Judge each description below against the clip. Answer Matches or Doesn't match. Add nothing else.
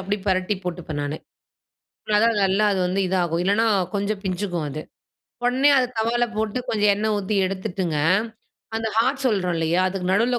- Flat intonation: Doesn't match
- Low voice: Doesn't match